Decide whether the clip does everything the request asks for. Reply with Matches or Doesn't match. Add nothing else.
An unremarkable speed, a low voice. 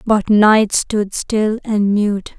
Doesn't match